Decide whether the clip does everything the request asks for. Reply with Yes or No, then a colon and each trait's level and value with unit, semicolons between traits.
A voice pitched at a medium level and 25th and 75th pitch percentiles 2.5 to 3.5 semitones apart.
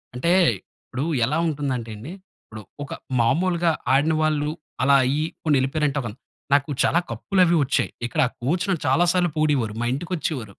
No: medium, 145 Hz; average, 4.1 semitones